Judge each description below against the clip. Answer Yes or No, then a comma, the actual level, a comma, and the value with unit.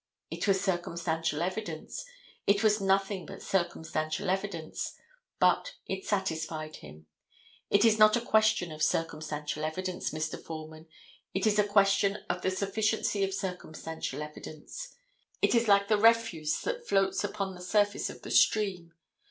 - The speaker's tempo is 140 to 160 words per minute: Yes, average, 145 wpm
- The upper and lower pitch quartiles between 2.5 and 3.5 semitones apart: No, average, 4.2 semitones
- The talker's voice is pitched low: No, high, 190 Hz